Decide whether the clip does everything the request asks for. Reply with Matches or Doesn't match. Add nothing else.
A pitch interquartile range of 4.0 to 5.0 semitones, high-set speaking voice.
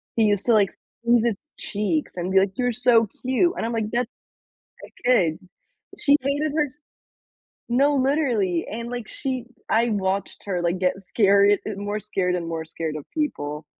Matches